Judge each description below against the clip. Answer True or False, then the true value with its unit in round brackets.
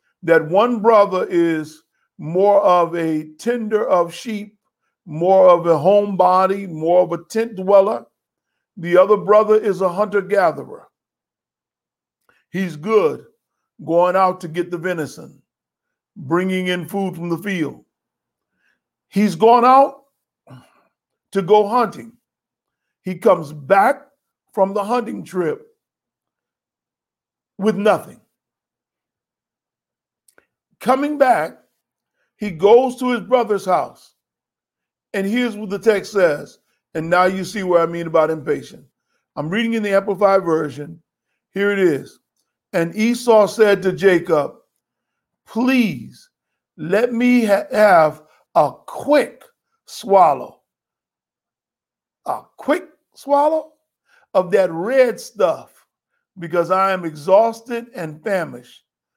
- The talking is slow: True (115 wpm)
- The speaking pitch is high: True (195 Hz)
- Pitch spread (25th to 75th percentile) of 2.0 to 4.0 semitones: False (4.6 semitones)